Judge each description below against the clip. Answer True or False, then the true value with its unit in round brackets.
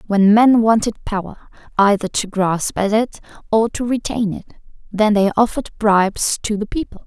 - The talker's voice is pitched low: False (210 Hz)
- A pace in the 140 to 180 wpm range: True (170 wpm)